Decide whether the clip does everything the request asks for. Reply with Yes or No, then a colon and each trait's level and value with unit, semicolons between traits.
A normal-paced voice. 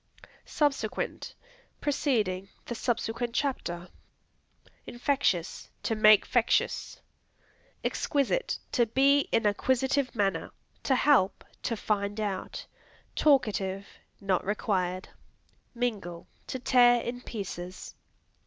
No: slow, 95 wpm